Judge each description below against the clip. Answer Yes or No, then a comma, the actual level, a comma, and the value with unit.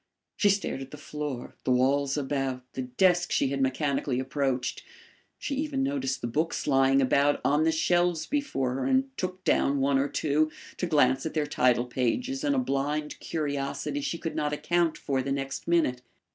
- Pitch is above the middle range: No, medium, 145 Hz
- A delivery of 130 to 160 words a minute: No, average, 185 wpm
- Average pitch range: Yes, average, 4.3 semitones